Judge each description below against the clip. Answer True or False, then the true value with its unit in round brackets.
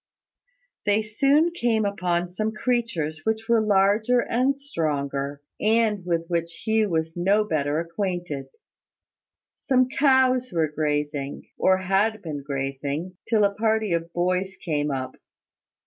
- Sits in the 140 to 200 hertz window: True (190 Hz)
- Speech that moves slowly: True (130 wpm)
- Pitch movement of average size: False (5.7 semitones)